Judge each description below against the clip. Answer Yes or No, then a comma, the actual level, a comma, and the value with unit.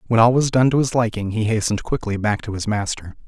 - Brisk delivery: Yes, fast, 255 wpm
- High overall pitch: No, low, 110 Hz